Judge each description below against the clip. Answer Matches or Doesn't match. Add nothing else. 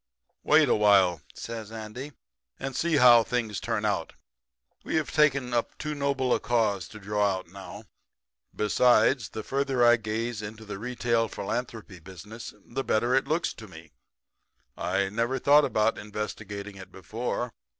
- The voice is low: Matches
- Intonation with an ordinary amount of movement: Matches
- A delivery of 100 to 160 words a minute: Matches